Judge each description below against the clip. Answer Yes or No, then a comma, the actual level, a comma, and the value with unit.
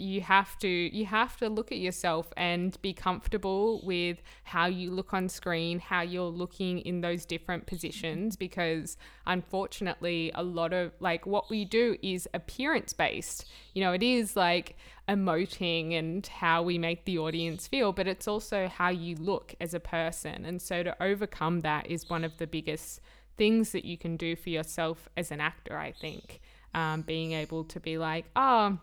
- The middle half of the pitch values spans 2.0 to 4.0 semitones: Yes, narrow, 2.5 semitones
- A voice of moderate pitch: Yes, medium, 175 Hz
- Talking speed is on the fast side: No, average, 185 wpm